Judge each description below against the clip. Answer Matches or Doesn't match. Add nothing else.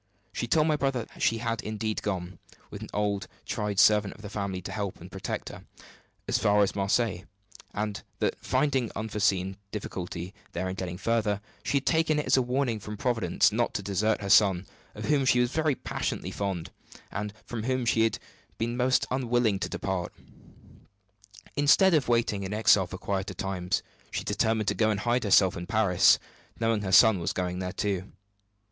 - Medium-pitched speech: Doesn't match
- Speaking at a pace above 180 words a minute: Matches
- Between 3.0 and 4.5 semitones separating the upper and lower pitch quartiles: Matches